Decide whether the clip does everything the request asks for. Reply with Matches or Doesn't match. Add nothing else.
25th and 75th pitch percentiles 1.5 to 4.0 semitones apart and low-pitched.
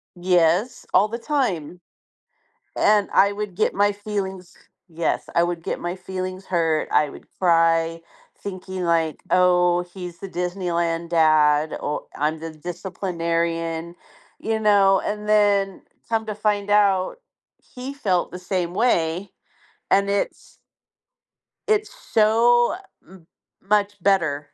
Doesn't match